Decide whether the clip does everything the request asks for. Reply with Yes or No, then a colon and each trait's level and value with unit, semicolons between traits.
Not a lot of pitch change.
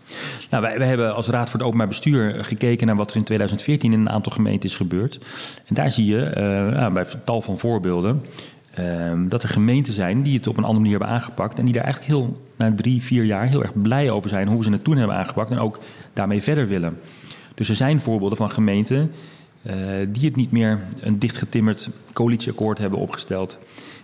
No: average, 3.7 semitones